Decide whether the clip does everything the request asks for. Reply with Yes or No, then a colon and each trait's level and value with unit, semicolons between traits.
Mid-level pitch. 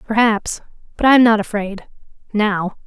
No: high, 215 Hz